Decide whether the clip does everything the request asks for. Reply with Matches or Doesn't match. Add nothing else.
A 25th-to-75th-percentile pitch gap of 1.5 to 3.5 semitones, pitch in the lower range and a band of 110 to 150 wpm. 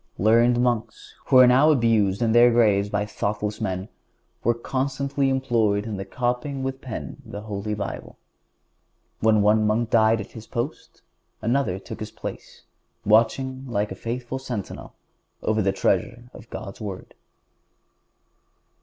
Matches